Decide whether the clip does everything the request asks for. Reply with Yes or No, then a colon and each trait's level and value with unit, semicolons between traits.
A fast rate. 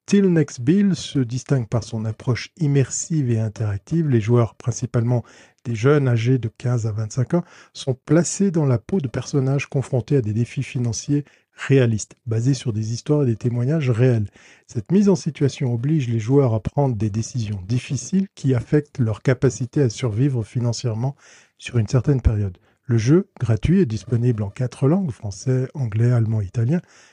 No: average, 175 wpm